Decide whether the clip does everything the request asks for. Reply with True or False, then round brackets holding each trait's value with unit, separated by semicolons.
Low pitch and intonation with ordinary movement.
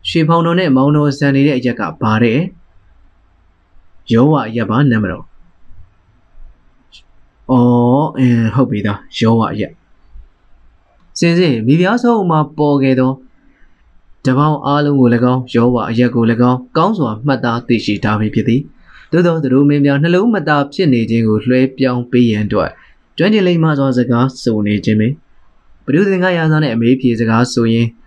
True (125 Hz; 4.9 semitones)